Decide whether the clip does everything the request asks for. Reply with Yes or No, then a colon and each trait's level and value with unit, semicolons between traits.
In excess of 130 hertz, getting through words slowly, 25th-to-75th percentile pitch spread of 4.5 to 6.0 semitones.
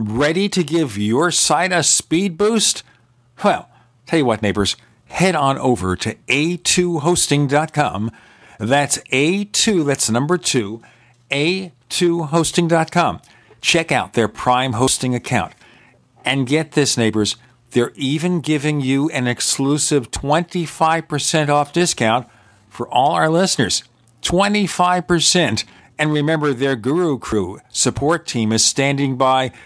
Yes: medium, 140 Hz; slow, 115 wpm; average, 5.2 semitones